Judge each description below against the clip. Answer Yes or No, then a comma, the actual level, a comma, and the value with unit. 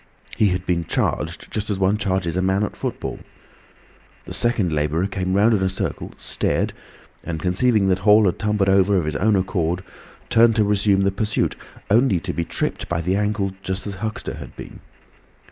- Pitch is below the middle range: Yes, very low, 95 Hz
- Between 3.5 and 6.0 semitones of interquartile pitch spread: No, narrow, 2.6 semitones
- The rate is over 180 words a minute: Yes, average, 190 wpm